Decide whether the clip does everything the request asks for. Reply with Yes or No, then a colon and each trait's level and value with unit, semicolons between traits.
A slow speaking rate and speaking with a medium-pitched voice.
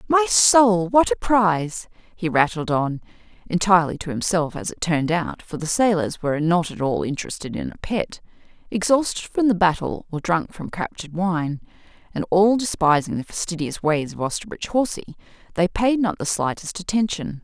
No: average, 170 wpm; medium, 180 Hz